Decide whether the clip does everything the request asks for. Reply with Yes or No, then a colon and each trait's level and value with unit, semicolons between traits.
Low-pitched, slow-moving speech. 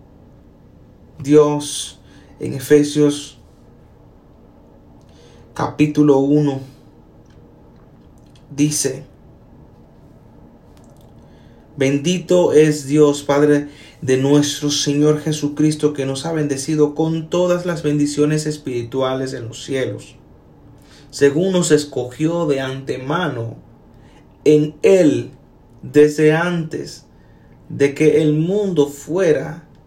No: medium, 145 Hz; slow, 80 wpm